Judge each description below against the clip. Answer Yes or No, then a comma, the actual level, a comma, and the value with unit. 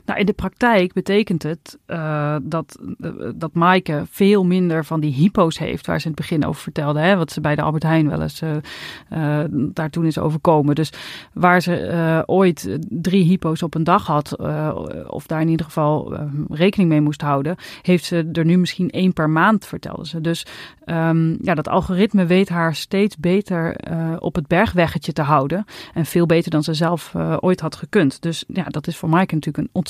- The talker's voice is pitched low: No, medium, 165 Hz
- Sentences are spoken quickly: Yes, fast, 210 wpm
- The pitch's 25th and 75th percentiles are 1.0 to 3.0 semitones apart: Yes, narrow, 2.6 semitones